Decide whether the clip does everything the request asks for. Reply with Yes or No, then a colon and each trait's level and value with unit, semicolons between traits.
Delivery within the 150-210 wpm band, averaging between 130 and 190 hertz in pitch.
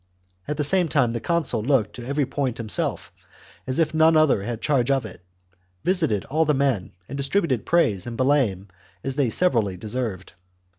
Yes: average, 185 wpm; low, 135 Hz